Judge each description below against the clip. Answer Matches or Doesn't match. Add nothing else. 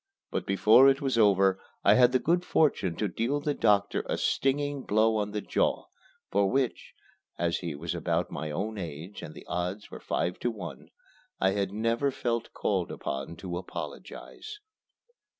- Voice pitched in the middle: Doesn't match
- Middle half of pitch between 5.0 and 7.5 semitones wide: Matches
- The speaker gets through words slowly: Doesn't match